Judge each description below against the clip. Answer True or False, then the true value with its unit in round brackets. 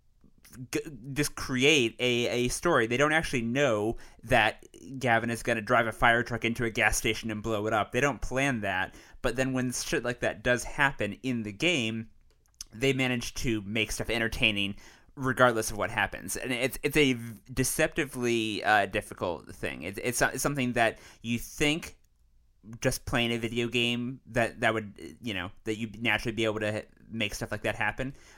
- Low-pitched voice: True (115 Hz)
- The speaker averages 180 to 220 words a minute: True (185 wpm)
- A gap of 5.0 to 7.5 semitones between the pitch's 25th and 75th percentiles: False (2.9 semitones)